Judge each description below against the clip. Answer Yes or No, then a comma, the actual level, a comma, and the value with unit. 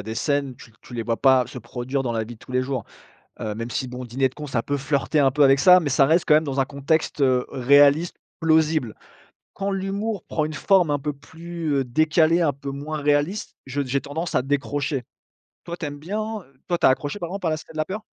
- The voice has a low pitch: No, medium, 145 Hz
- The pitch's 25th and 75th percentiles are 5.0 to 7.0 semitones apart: No, average, 3.5 semitones